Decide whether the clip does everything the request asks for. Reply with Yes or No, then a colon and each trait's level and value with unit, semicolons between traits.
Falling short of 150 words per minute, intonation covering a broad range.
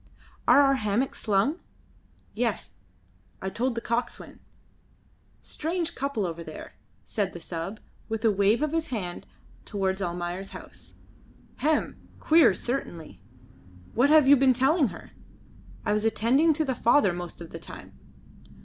Yes: average, 140 wpm; wide, 6.6 semitones